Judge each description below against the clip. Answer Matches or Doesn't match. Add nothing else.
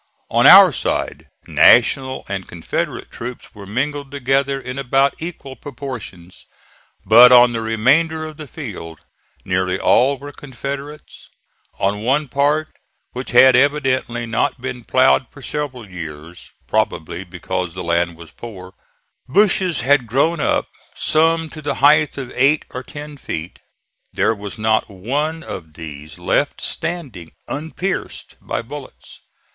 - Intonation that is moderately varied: Doesn't match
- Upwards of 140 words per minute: Doesn't match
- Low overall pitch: Matches